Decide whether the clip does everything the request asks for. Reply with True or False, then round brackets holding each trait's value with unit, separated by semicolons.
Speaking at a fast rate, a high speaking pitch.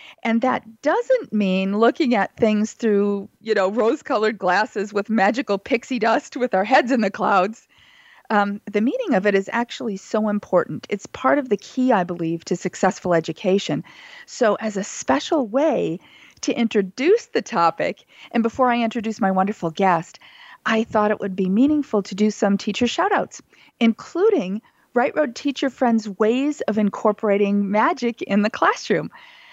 False (165 wpm; 220 Hz)